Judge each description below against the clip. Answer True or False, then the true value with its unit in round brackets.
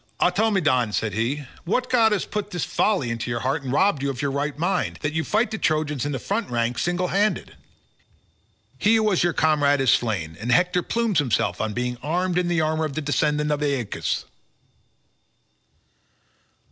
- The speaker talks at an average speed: True (185 wpm)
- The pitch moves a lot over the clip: True (5.8 semitones)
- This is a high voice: False (150 Hz)